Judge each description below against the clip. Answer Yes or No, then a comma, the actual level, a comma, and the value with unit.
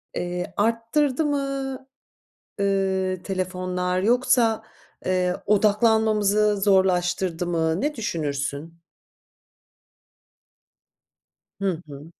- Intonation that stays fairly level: No, average, 3.9 semitones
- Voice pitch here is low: No, high, 195 Hz